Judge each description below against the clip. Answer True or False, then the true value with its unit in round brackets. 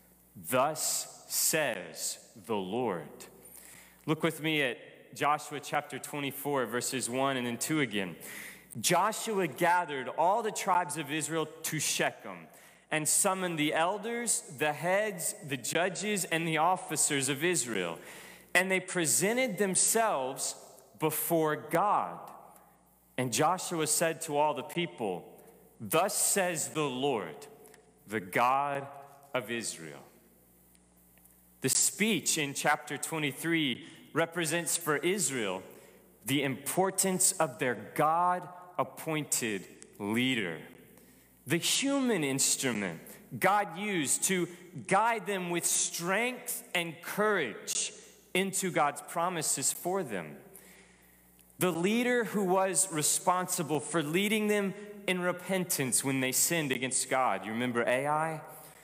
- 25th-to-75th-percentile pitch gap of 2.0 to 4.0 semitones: False (4.9 semitones)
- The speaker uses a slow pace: True (110 wpm)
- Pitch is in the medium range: True (160 Hz)